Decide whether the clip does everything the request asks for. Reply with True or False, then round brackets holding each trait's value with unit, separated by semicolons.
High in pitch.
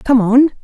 True (250 Hz)